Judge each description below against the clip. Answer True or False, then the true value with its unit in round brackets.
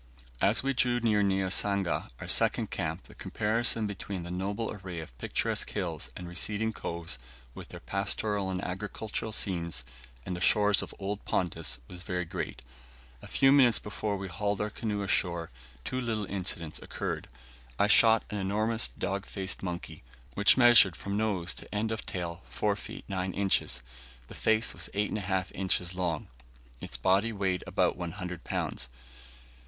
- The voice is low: True (100 Hz)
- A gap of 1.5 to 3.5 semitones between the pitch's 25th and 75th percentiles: True (2.9 semitones)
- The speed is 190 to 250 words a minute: False (160 wpm)